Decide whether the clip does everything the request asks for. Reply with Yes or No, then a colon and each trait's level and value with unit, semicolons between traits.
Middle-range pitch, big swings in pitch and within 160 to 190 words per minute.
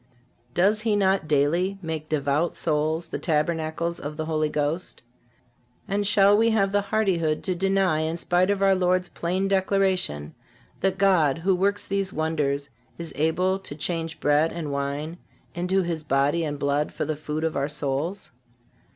No: medium, 170 Hz; average, 4.0 semitones; average, 165 wpm